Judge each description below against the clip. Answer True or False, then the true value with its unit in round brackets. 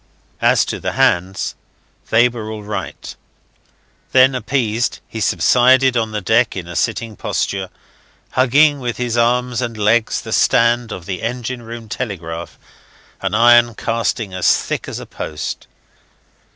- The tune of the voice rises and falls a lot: False (2.8 semitones)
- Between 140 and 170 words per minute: True (145 wpm)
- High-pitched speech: False (115 Hz)